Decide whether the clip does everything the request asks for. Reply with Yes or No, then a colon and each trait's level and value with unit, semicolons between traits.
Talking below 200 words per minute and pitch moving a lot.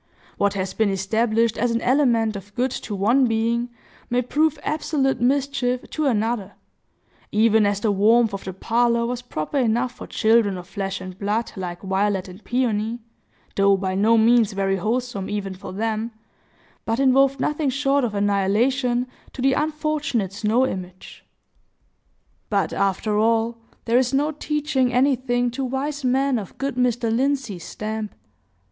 No: average, 150 wpm; average, 4.0 semitones